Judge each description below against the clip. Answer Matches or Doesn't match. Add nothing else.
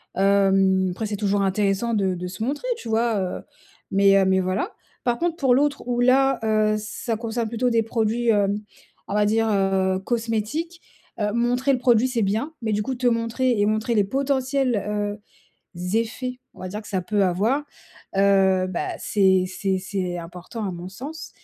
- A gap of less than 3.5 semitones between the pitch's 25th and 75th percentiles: Doesn't match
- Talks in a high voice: Matches